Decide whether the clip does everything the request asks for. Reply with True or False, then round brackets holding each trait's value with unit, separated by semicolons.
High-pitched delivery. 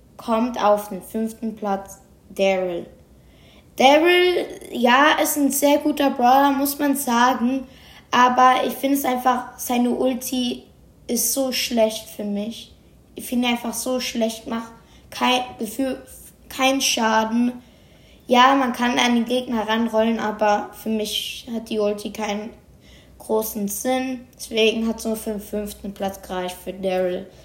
True (235 Hz)